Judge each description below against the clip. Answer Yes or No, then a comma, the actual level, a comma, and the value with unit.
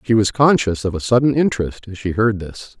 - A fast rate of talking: Yes, fast, 235 wpm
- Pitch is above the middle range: No, low, 110 Hz